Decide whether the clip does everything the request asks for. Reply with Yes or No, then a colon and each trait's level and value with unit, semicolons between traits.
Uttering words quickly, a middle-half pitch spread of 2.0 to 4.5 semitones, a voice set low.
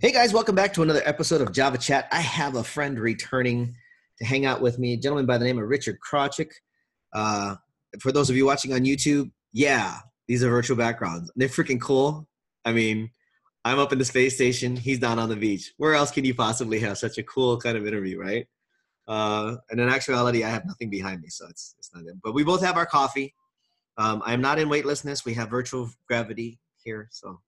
Yes: fast, 220 wpm; average, 3.6 semitones; low, 125 Hz